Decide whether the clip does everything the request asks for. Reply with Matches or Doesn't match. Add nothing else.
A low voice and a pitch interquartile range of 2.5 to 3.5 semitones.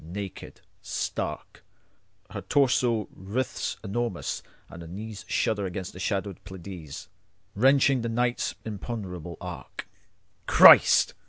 Doesn't match